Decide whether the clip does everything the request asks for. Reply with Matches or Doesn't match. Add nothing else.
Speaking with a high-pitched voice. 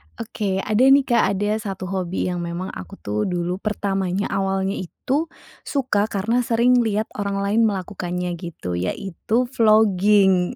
Matches